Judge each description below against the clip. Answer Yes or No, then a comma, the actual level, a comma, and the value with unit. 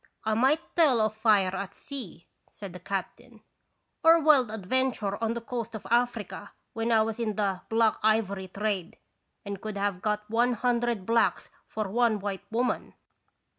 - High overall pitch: Yes, high, 220 Hz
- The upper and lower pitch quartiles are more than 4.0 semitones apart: No, average, 2.9 semitones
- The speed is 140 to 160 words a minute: No, average, 175 wpm